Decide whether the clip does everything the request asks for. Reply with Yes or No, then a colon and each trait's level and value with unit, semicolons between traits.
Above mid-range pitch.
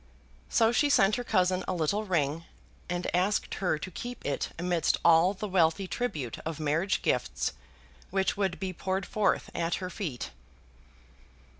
No: medium, 180 Hz